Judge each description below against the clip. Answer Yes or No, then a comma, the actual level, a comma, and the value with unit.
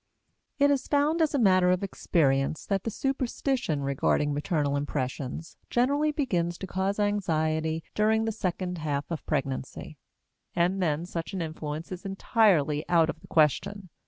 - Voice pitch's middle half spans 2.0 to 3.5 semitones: No, average, 5.2 semitones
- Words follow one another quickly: No, average, 155 wpm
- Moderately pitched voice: Yes, medium, 175 Hz